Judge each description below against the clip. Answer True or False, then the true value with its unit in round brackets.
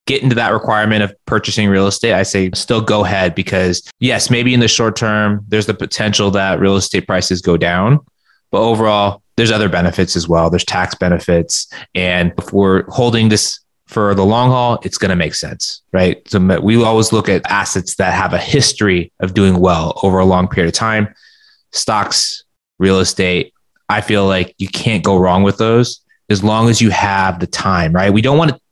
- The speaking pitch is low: True (100 Hz)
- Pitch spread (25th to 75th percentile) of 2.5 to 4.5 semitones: True (3.1 semitones)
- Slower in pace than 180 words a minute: False (205 wpm)